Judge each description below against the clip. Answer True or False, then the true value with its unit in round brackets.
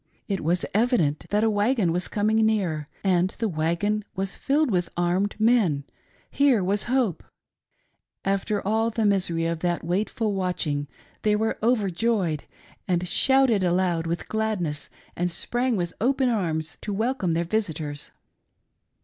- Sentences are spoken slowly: False (145 wpm)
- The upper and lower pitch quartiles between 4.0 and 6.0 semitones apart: True (4.3 semitones)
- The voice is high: True (195 Hz)